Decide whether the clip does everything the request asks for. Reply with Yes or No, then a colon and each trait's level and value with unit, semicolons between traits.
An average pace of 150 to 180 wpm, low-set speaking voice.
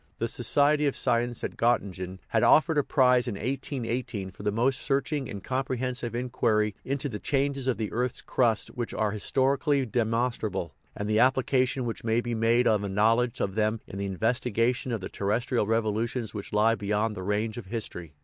No: average, 190 wpm; low, 115 Hz